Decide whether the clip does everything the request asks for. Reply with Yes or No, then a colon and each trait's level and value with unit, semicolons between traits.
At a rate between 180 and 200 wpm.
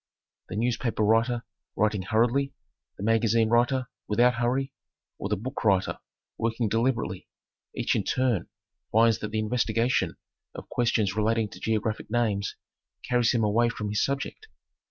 No: average, 140 wpm